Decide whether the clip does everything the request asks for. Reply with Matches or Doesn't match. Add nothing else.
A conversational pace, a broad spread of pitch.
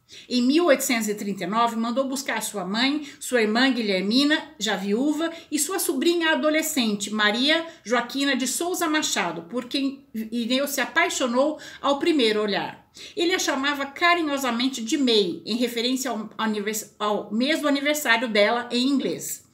Doesn't match